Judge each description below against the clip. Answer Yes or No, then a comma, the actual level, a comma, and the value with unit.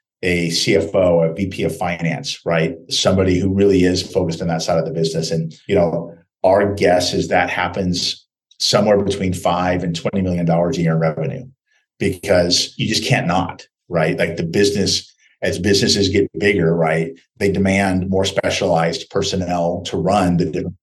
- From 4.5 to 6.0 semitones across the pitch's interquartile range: No, narrow, 2.4 semitones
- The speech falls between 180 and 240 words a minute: No, average, 170 wpm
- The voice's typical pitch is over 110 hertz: No, very low, 90 Hz